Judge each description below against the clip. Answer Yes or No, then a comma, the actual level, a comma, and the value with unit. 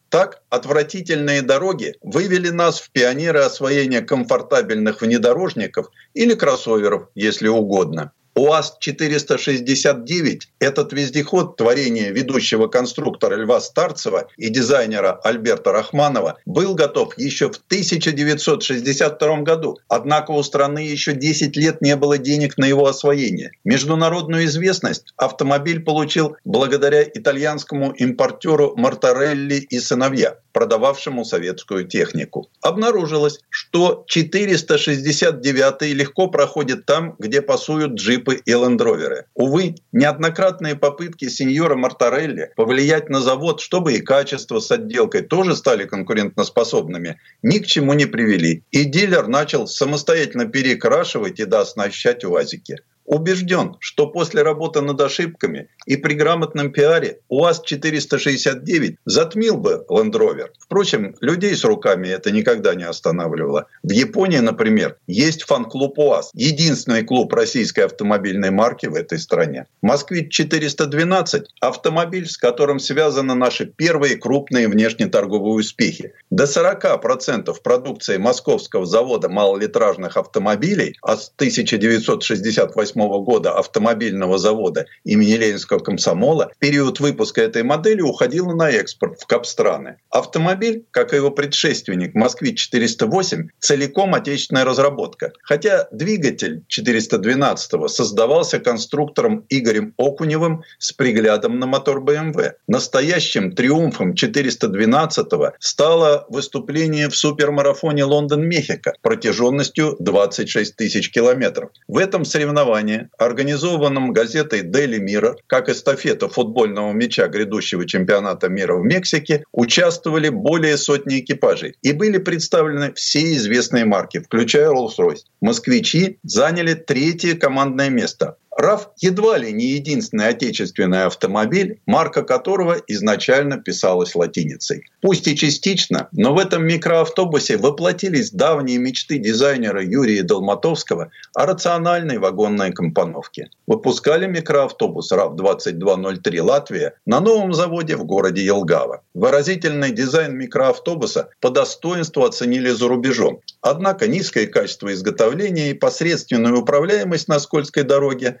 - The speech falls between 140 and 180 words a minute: No, slow, 110 wpm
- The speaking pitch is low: No, medium, 155 Hz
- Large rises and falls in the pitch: Yes, wide, 5.7 semitones